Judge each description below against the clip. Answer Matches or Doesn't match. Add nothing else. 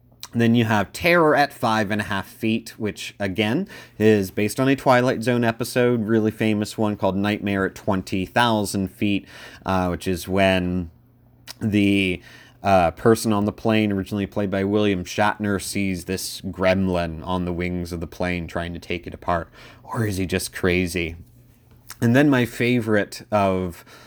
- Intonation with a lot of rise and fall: Doesn't match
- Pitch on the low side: Matches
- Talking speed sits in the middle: Matches